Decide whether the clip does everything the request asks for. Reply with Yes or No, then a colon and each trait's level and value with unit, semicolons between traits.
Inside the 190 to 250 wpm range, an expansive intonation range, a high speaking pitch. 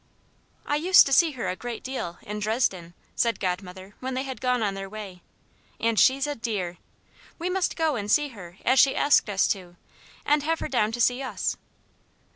Yes: average, 200 wpm; wide, 5.8 semitones; high, 230 Hz